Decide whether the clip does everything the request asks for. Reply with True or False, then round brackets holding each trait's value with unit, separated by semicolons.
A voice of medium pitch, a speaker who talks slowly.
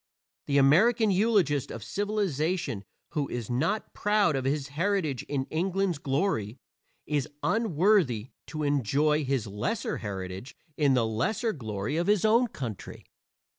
True (150 Hz; 130 wpm)